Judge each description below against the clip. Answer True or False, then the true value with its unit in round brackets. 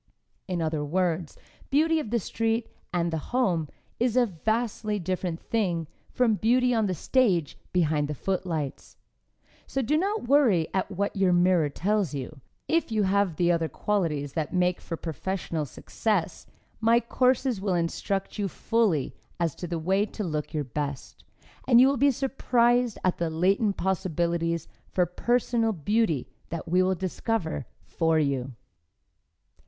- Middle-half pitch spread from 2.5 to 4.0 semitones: False (5.6 semitones)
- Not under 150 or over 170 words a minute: True (155 wpm)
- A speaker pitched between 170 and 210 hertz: True (185 Hz)